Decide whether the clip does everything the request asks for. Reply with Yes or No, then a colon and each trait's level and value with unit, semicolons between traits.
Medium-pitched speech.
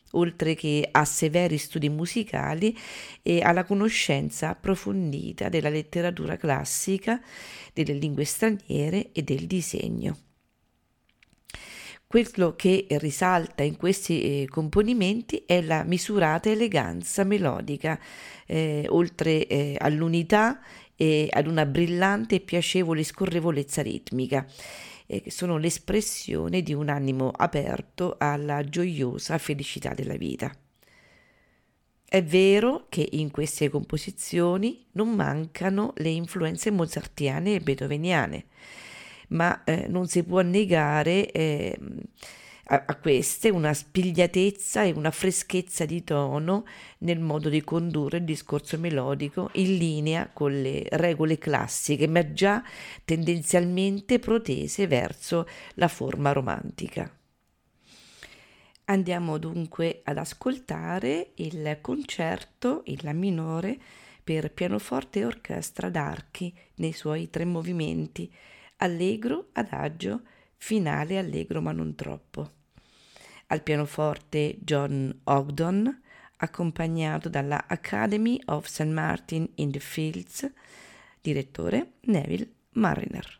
Yes: medium, 165 Hz